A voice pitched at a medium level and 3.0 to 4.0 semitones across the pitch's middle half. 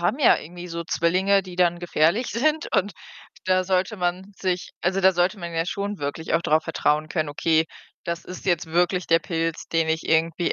No: medium, 175 Hz; narrow, 2.4 semitones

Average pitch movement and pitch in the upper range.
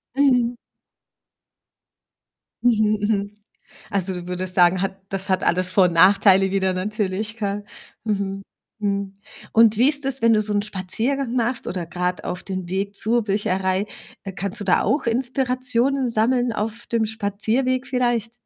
Yes: average, 3.6 semitones; high, 210 Hz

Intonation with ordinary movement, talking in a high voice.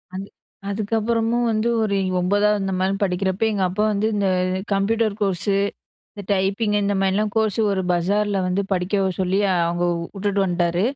No: narrow, 1.9 semitones; high, 200 Hz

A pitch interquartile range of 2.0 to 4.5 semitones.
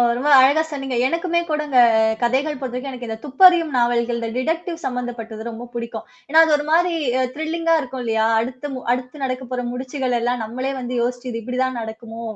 Yes: average, 3.7 semitones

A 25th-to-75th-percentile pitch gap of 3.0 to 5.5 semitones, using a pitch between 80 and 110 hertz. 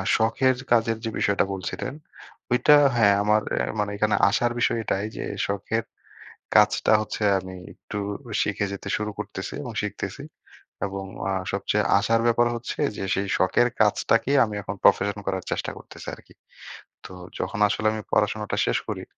No: narrow, 2.4 semitones; low, 105 Hz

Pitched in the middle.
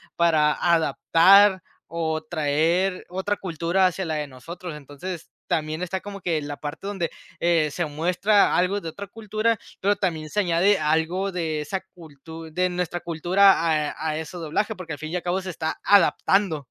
Yes: medium, 170 Hz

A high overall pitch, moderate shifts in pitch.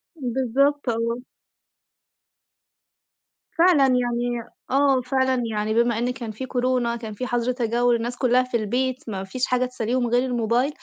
No: high, 245 Hz; narrow, 1.6 semitones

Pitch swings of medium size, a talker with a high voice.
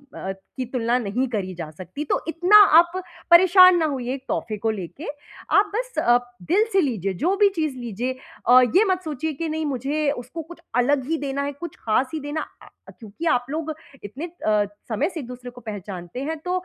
No: wide, 5.7 semitones; very high, 275 Hz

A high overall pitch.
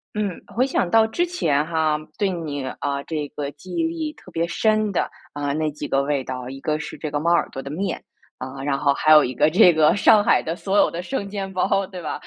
No: medium, 160 Hz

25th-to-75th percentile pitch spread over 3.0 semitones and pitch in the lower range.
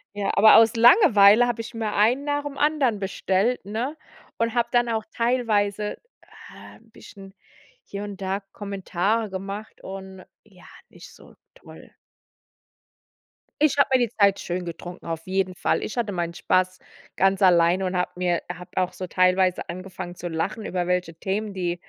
No: average, 3.8 semitones; high, 200 Hz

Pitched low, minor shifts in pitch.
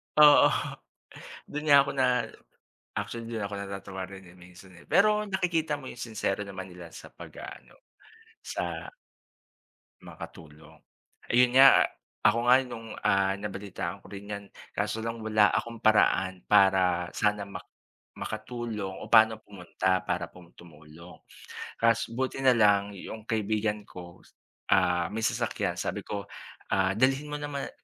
No: low, 105 Hz; average, 4.0 semitones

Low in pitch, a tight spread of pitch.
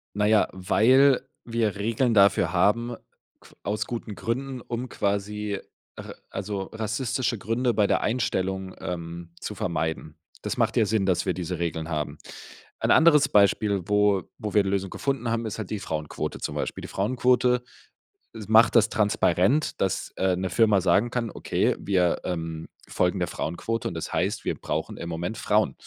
No: low, 105 Hz; average, 3.8 semitones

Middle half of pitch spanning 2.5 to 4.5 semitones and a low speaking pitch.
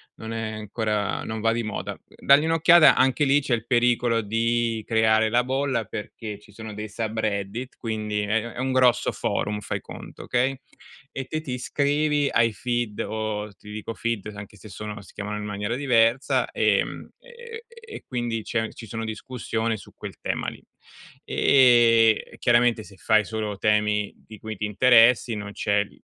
Yes: average, 2.9 semitones; low, 115 Hz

